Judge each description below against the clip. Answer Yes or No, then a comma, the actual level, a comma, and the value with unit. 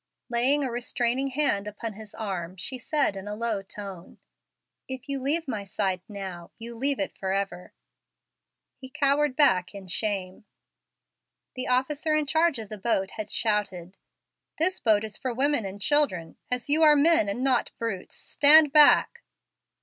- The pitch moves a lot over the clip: Yes, wide, 6.1 semitones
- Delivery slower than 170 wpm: Yes, average, 160 wpm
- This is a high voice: Yes, high, 235 Hz